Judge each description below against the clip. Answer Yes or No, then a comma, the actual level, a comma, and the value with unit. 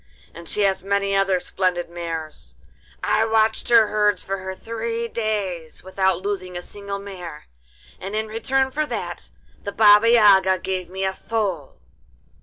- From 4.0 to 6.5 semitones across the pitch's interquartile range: No, average, 2.8 semitones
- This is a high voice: Yes, high, 195 Hz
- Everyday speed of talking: Yes, average, 150 wpm